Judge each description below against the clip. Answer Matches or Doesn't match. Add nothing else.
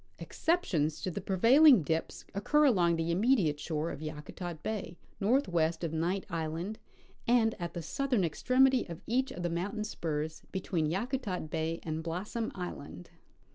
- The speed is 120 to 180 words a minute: Matches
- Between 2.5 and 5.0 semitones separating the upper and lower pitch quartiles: Doesn't match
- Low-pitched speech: Doesn't match